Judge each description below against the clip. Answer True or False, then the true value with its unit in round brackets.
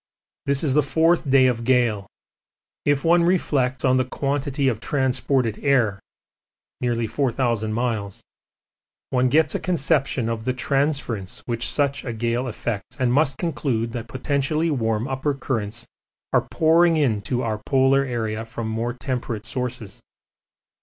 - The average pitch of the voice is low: True (130 Hz)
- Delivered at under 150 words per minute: True (140 wpm)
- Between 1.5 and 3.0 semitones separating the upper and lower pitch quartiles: False (3.4 semitones)